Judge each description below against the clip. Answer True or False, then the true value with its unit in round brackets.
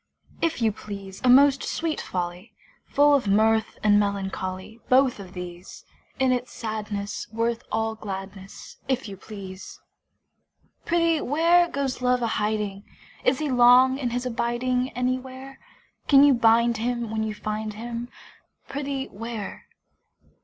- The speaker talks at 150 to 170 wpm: False (140 wpm)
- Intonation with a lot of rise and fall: False (3.8 semitones)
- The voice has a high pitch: True (235 Hz)